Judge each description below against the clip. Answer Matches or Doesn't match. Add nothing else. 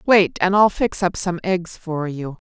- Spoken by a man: Doesn't match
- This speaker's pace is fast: Matches